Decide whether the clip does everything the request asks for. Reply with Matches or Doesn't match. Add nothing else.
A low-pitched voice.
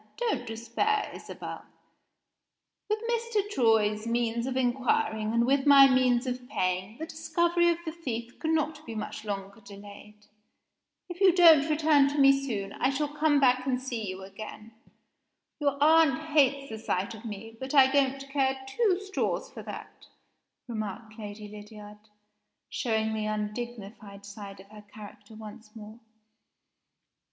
Doesn't match